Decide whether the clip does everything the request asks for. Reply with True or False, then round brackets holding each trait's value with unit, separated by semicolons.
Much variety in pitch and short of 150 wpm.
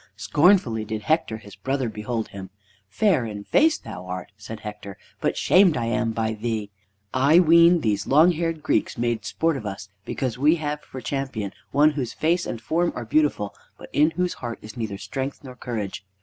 False (6.4 semitones; 190 wpm)